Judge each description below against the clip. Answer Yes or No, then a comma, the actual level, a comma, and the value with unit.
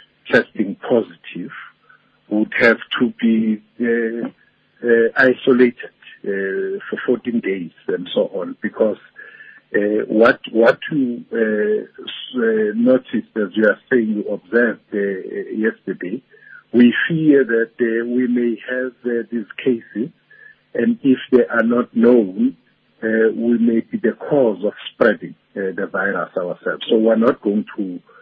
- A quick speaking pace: No, average, 140 wpm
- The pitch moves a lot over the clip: No, narrow, 2.5 semitones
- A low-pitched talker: Yes, low, 120 Hz